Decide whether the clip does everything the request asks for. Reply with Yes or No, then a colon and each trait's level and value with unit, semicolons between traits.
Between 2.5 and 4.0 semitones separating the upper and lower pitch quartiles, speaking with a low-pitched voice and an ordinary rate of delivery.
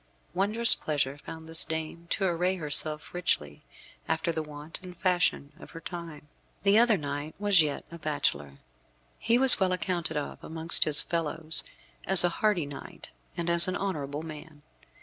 No: average, 3.3 semitones; medium, 165 Hz; average, 165 wpm